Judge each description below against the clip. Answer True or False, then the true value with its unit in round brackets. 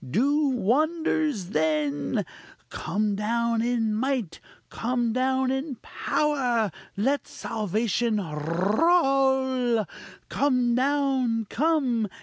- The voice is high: True (240 Hz)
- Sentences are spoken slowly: True (85 wpm)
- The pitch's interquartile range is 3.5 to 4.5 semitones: True (4.2 semitones)